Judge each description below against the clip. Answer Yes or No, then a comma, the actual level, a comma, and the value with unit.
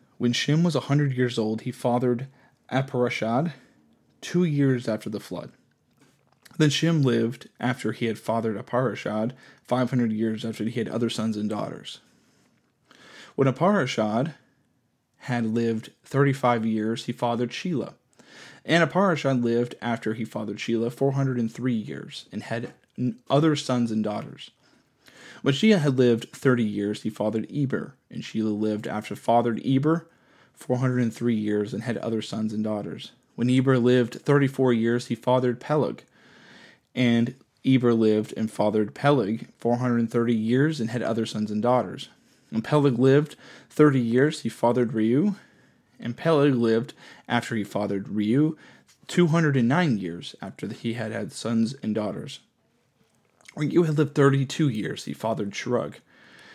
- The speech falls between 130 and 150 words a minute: Yes, average, 145 wpm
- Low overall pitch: Yes, low, 120 Hz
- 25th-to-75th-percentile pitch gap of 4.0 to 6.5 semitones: No, average, 3.3 semitones